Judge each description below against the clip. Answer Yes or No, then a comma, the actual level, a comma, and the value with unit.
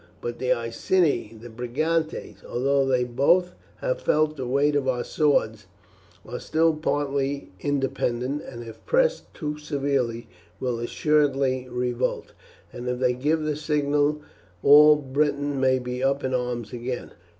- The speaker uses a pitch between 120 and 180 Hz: Yes, low, 135 Hz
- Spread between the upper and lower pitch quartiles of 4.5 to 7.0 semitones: No, average, 3.2 semitones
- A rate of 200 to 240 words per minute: No, average, 140 wpm